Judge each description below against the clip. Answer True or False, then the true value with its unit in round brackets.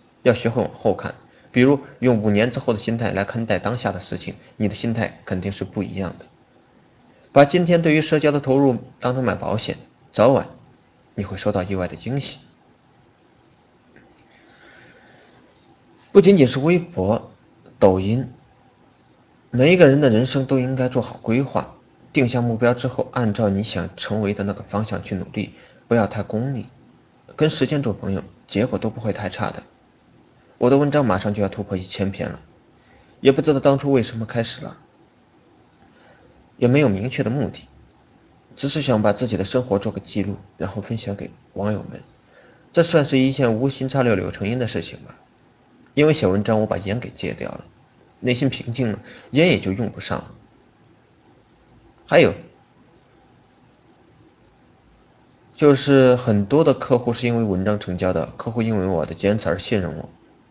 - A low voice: True (115 Hz)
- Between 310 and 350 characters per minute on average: False (245 characters per minute)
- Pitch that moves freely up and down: False (4.8 semitones)